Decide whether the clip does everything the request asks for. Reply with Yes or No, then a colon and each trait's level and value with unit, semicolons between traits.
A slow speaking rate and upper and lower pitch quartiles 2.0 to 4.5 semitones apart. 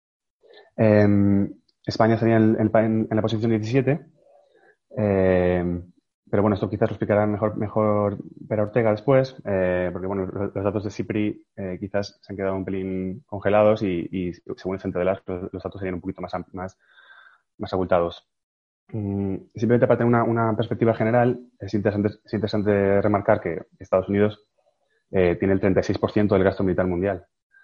No: average, 175 wpm; narrow, 2.6 semitones